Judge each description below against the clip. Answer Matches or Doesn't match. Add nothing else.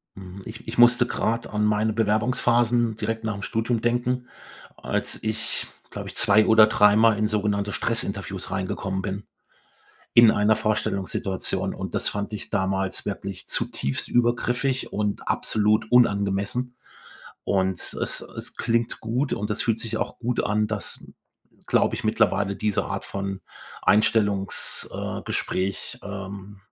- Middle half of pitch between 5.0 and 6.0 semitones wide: Doesn't match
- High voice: Doesn't match